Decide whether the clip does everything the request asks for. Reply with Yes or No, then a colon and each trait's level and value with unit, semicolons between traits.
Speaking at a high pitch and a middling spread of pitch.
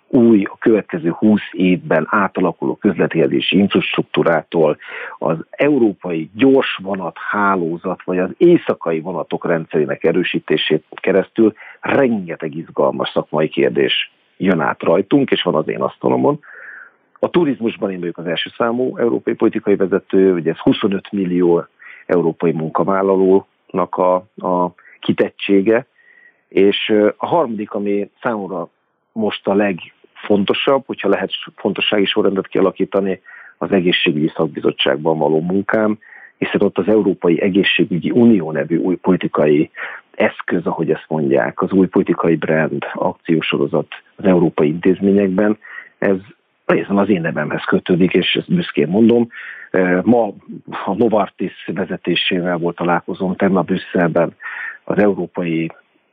No: very low, 95 Hz; average, 3.1 semitones